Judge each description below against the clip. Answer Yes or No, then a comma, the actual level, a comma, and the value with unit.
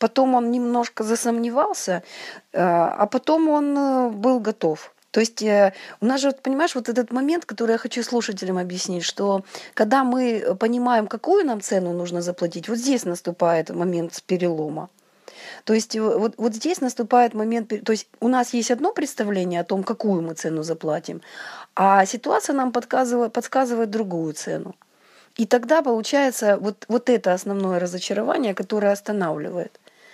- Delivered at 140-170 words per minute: Yes, average, 145 wpm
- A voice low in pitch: No, high, 225 Hz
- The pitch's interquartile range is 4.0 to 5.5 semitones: Yes, average, 4.7 semitones